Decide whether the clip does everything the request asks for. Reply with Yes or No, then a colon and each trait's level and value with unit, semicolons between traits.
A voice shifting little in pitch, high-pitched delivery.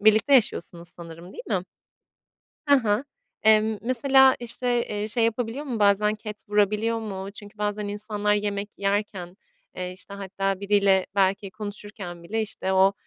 Yes: narrow, 1.9 semitones; high, 210 Hz